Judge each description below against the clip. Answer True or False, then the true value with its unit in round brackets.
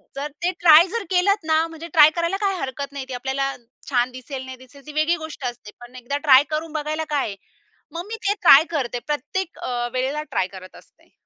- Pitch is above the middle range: True (290 Hz)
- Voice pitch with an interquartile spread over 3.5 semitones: True (4.2 semitones)